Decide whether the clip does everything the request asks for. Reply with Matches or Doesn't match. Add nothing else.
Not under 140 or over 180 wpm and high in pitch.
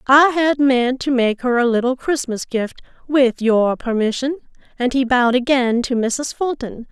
Matches